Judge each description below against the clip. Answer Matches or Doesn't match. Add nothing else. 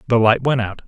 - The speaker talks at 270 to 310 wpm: Matches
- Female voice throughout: Doesn't match